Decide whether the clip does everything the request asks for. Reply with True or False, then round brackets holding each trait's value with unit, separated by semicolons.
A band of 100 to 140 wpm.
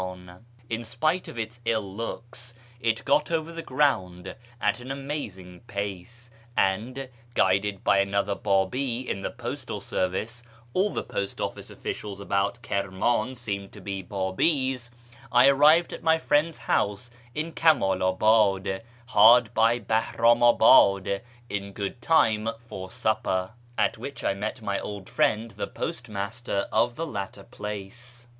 True (135 wpm)